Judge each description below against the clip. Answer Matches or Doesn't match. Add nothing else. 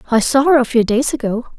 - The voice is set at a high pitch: Matches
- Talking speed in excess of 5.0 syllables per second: Matches